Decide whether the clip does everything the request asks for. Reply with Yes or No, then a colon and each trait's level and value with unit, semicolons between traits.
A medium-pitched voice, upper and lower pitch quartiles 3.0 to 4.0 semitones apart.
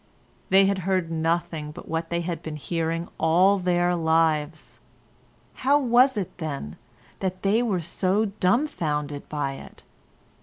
Yes: medium, 170 Hz; average, 3.3 semitones